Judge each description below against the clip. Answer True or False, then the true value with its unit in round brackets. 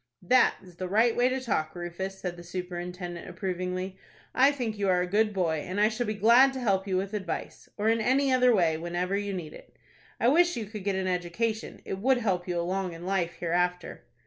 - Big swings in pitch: False (3.9 semitones)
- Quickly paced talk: True (225 wpm)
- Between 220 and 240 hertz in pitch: False (190 Hz)